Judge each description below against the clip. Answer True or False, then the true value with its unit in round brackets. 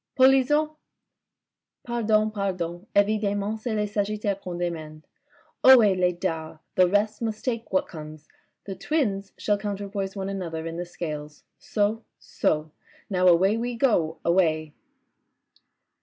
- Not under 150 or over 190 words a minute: False (140 wpm)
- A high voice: True (195 Hz)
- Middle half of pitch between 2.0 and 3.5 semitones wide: False (3.9 semitones)